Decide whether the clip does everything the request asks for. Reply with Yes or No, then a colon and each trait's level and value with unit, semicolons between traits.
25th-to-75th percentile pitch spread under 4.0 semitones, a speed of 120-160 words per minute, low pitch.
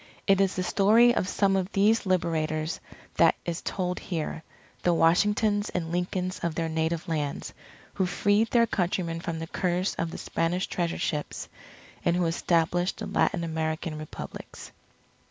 No: average, 2.9 semitones; average, 155 wpm; medium, 175 Hz